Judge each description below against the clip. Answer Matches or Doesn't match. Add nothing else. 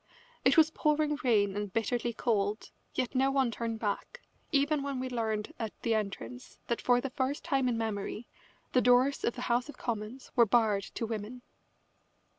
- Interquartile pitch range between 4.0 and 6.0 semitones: Doesn't match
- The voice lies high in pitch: Matches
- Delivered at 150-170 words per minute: Doesn't match